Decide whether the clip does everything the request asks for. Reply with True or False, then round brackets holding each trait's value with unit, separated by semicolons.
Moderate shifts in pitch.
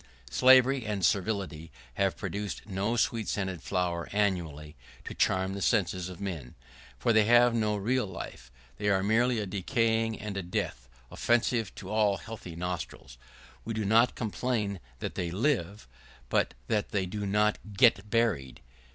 True (3.5 semitones)